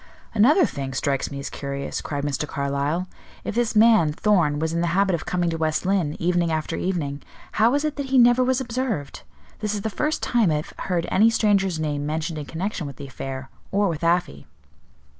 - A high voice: No, medium, 170 Hz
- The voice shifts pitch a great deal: Yes, wide, 6.5 semitones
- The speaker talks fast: Yes, fast, 210 wpm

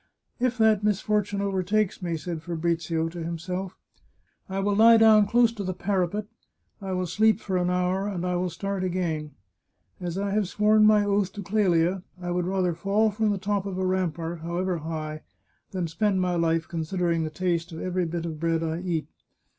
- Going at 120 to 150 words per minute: No, average, 195 wpm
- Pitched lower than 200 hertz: Yes, medium, 185 Hz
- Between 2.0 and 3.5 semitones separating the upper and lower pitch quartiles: Yes, average, 3.1 semitones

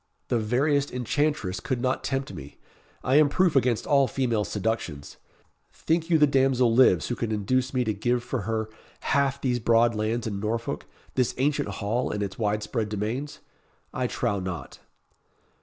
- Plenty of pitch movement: No, average, 4.0 semitones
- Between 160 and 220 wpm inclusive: Yes, average, 170 wpm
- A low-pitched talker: Yes, low, 120 Hz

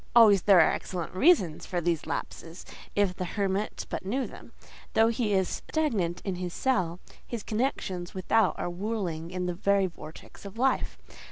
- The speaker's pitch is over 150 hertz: Yes, high, 190 Hz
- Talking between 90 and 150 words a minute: No, average, 170 wpm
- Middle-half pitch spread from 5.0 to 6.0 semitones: No, average, 3.7 semitones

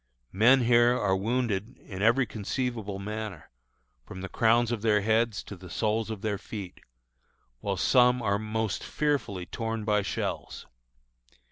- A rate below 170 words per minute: Yes, average, 145 wpm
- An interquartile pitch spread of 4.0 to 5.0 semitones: No, average, 2.9 semitones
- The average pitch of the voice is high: No, low, 110 Hz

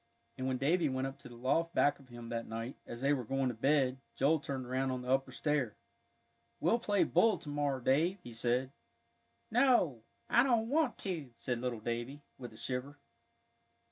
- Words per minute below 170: No, average, 195 wpm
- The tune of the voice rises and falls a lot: No, average, 3.6 semitones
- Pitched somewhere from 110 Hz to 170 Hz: Yes, low, 135 Hz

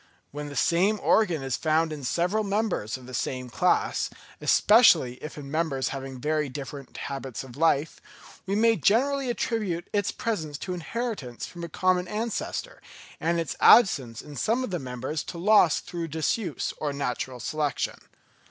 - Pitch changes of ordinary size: No, wide, 6.7 semitones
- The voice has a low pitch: No, medium, 160 Hz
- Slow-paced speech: No, average, 160 wpm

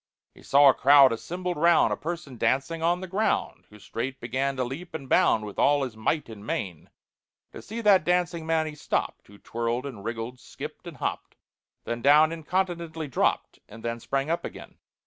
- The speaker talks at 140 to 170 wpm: No, average, 190 wpm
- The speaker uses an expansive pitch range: Yes, wide, 6.1 semitones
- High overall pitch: No, medium, 140 Hz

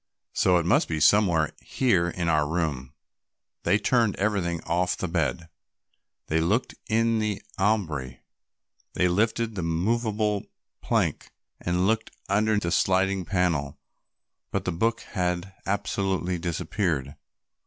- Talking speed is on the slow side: Yes, slow, 125 wpm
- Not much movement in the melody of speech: No, average, 3.9 semitones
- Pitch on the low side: Yes, very low, 90 Hz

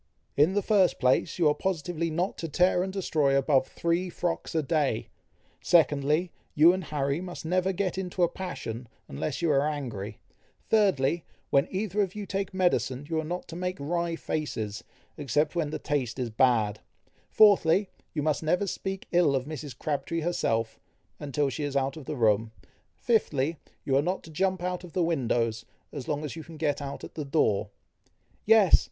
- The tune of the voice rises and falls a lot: No, average, 4.5 semitones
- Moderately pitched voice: Yes, medium, 155 Hz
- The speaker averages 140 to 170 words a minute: No, average, 185 wpm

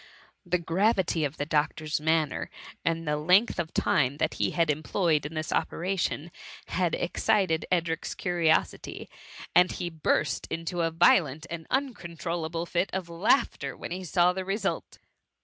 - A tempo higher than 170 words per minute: No, average, 150 wpm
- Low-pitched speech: No, medium, 170 Hz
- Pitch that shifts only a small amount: Yes, narrow, 2.3 semitones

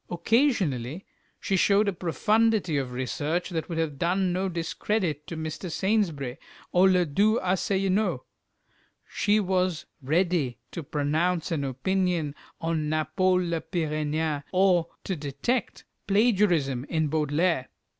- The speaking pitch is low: No, medium, 170 Hz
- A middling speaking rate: No, slow, 125 wpm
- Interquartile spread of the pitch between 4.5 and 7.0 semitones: No, average, 4.0 semitones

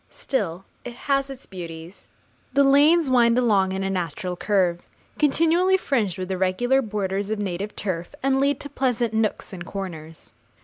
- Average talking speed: Yes, average, 160 wpm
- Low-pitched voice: No, high, 210 Hz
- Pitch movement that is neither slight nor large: No, wide, 6.4 semitones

